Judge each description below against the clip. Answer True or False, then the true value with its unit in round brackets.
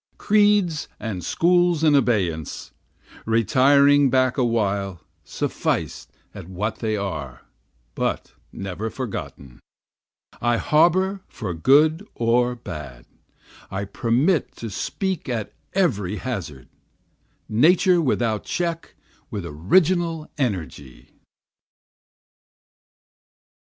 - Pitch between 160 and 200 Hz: False (120 Hz)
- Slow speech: True (90 wpm)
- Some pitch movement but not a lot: False (8.3 semitones)